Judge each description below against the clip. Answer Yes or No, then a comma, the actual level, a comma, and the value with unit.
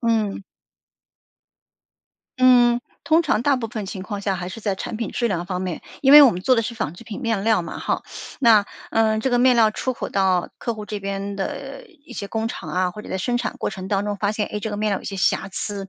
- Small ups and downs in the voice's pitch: No, average, 3.4 semitones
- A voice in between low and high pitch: No, high, 215 Hz